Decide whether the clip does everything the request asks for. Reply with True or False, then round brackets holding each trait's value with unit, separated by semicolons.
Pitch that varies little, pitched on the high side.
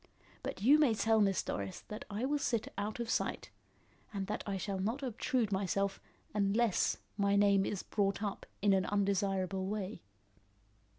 True (2.1 semitones; 200 Hz)